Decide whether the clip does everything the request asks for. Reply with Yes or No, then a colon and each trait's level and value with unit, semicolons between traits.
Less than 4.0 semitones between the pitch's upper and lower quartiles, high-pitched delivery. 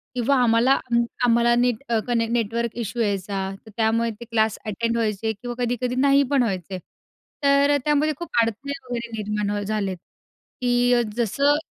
Yes: narrow, 2.4 semitones; high, 235 Hz